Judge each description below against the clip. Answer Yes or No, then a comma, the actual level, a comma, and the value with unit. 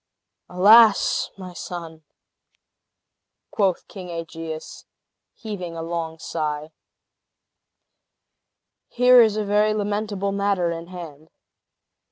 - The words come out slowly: Yes, slow, 90 wpm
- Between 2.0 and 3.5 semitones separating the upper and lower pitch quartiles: No, average, 3.9 semitones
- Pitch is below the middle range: No, medium, 180 Hz